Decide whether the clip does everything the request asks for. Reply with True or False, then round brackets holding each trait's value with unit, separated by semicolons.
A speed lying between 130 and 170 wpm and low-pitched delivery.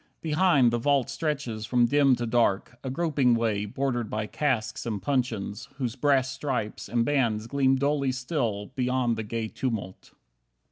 True (155 wpm; 125 Hz)